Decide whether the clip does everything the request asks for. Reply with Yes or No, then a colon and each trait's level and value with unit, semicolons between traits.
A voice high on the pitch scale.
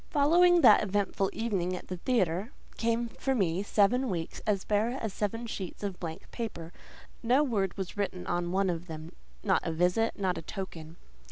Yes: high, 195 Hz